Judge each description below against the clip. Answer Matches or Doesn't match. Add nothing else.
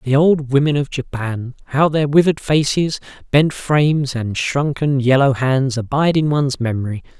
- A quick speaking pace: Doesn't match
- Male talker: Matches